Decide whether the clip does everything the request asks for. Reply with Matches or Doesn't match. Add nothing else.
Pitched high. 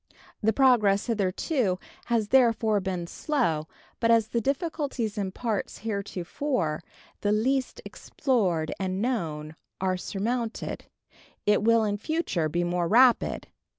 Matches